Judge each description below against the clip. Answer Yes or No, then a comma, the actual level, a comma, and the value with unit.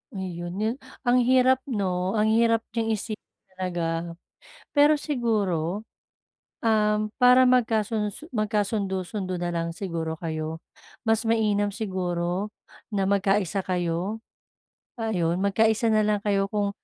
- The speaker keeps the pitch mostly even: No, average, 3.6 semitones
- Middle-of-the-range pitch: No, high, 205 Hz